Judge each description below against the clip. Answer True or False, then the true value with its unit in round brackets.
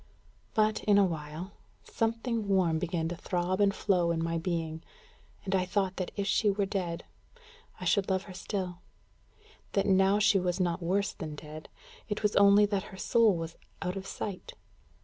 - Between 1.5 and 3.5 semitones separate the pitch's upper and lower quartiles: True (2.9 semitones)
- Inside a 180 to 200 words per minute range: True (185 wpm)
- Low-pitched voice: False (190 Hz)